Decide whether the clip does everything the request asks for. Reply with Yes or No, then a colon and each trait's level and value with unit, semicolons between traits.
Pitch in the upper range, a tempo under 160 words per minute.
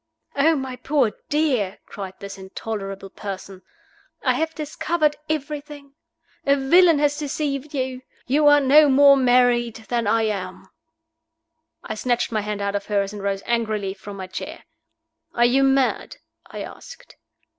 Yes: very high, 250 Hz; average, 145 wpm